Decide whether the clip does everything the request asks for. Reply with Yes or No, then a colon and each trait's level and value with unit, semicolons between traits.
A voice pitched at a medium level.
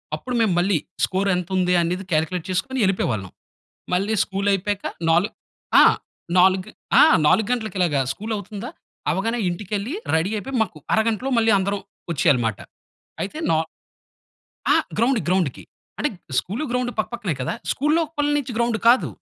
No: high, 200 Hz